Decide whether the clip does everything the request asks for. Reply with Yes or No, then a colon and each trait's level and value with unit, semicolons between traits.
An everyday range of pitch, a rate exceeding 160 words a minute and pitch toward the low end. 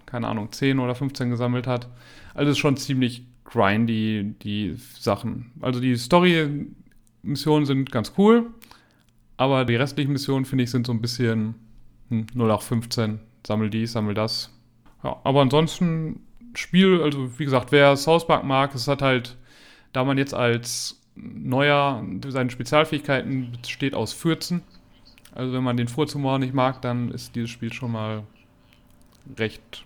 No: average, 3.2 semitones; average, 155 wpm; low, 125 Hz